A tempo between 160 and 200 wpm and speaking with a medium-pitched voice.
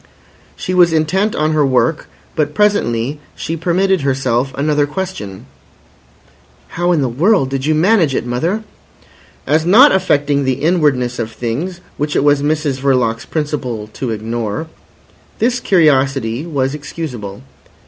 No: average, 140 wpm; medium, 145 Hz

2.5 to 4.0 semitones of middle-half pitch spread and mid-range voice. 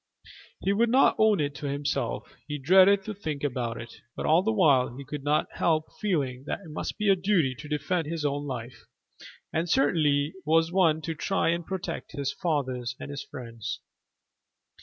No: average, 4.6 semitones; medium, 150 Hz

